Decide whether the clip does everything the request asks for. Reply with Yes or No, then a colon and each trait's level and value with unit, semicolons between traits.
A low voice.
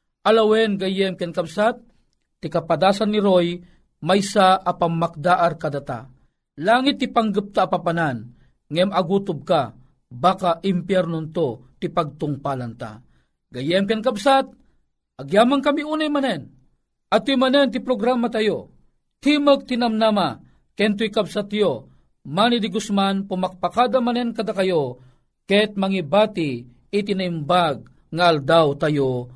No: high, 190 Hz